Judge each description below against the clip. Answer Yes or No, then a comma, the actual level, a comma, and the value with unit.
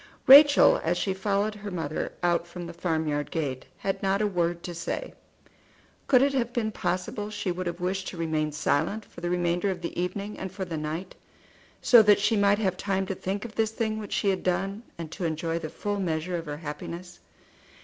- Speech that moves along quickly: Yes, fast, 210 wpm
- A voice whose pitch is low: No, medium, 185 Hz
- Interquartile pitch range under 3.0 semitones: No, average, 3.3 semitones